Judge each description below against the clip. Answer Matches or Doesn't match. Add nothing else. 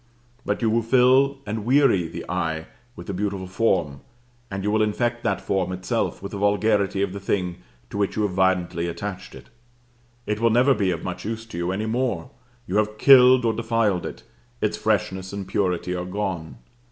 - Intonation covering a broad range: Doesn't match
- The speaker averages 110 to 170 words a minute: Doesn't match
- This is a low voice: Matches